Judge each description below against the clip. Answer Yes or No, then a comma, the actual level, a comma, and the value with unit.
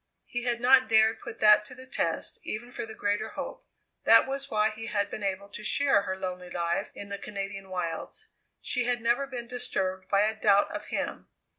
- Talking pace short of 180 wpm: No, fast, 205 wpm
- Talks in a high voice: Yes, high, 215 Hz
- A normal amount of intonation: Yes, average, 3.6 semitones